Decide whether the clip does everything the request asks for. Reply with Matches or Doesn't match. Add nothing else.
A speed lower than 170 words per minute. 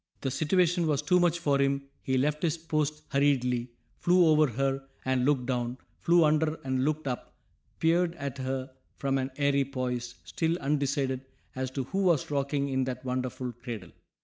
Doesn't match